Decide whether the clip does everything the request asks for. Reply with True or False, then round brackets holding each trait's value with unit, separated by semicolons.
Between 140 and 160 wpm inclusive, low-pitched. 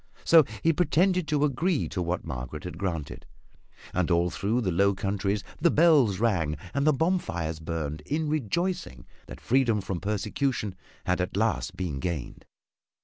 True (155 wpm; 100 Hz)